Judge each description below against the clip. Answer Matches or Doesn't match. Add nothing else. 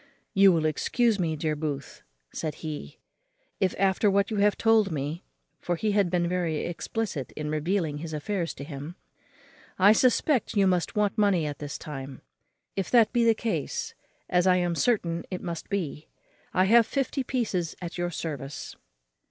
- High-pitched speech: Doesn't match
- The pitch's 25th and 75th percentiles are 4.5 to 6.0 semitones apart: Matches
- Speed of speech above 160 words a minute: Matches